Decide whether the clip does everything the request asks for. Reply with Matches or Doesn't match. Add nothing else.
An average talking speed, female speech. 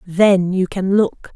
Matches